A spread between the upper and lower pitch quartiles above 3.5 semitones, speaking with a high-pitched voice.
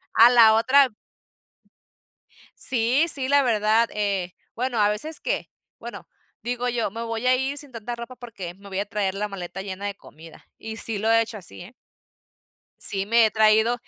No: average, 3.2 semitones; high, 225 Hz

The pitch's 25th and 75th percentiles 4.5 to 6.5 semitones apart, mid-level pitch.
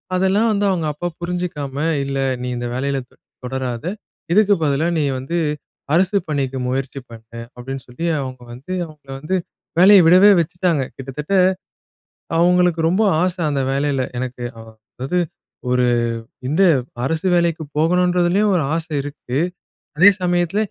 Yes: average, 5.0 semitones; medium, 160 Hz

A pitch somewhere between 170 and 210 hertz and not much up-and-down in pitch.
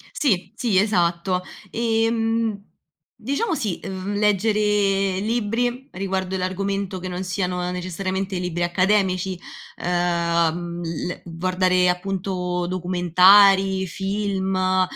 Yes: medium, 185 Hz; narrow, 2.2 semitones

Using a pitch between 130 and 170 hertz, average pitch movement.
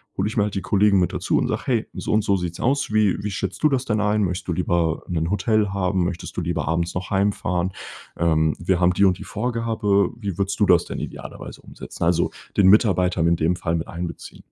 No: very low, 95 Hz; average, 3.1 semitones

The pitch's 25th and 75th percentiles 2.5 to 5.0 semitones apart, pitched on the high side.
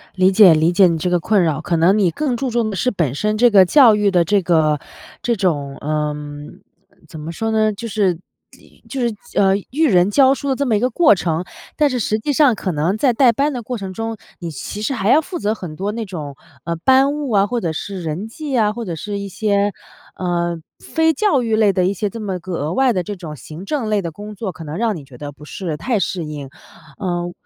No: wide, 5.4 semitones; high, 200 Hz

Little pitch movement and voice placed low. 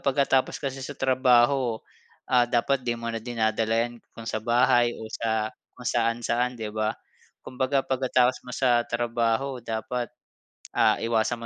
Yes: narrow, 2.0 semitones; low, 120 Hz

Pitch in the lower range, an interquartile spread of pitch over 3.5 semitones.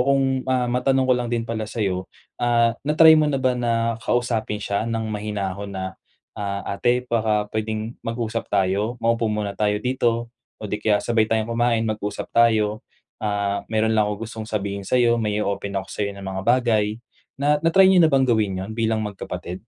No: low, 110 Hz; narrow, 2.6 semitones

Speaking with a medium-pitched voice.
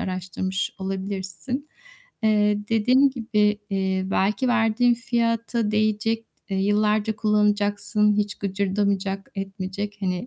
No: high, 210 Hz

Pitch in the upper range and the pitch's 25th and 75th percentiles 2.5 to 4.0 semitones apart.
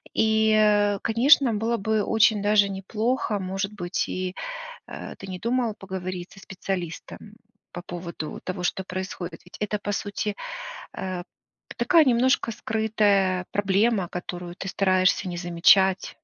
Yes: high, 195 Hz; average, 2.9 semitones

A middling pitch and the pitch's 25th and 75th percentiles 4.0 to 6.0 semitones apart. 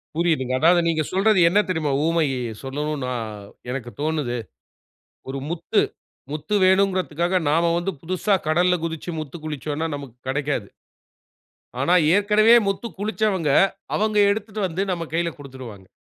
Yes: medium, 165 Hz; average, 4.6 semitones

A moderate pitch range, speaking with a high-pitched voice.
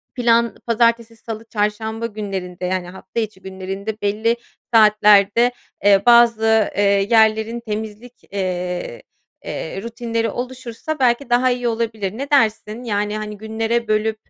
No: narrow, 2.3 semitones; high, 220 Hz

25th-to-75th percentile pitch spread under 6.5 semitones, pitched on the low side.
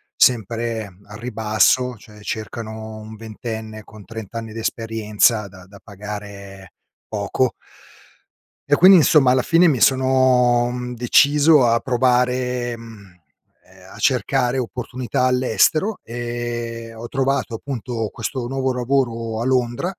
Yes: narrow, 2.6 semitones; low, 120 Hz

